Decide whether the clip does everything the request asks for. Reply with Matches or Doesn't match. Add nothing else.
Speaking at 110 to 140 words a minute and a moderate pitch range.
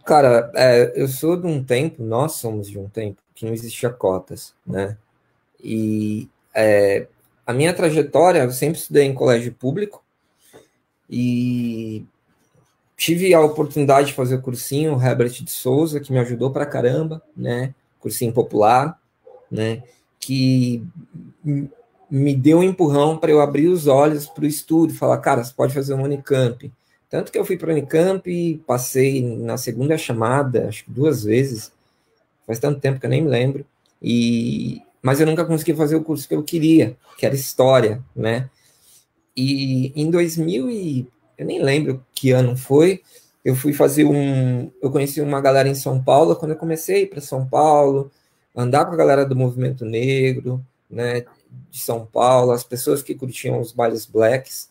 Doesn't match